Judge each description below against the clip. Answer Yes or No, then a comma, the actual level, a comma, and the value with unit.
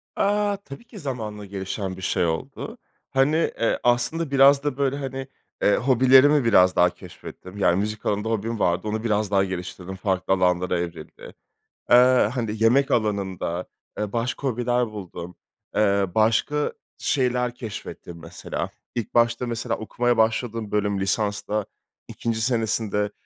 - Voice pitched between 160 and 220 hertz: No, low, 110 Hz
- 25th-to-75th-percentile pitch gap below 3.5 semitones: No, average, 4.2 semitones